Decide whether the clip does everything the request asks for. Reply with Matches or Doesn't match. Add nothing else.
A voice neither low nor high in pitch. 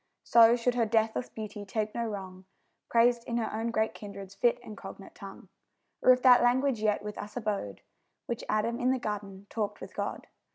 Doesn't match